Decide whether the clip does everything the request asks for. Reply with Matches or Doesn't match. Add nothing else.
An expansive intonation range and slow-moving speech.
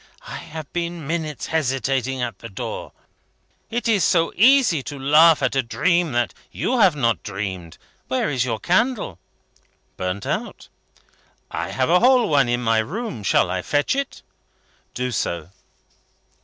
Doesn't match